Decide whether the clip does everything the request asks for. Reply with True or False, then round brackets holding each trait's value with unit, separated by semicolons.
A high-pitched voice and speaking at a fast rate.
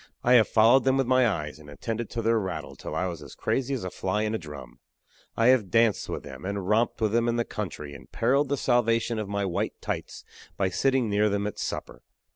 False (110 Hz; 240 wpm)